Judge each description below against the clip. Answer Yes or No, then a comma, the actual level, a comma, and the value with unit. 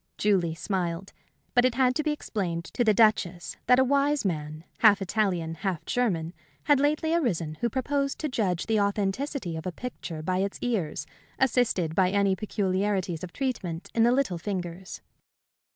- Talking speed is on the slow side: No, average, 170 wpm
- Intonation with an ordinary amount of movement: No, wide, 6.2 semitones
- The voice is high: Yes, high, 200 Hz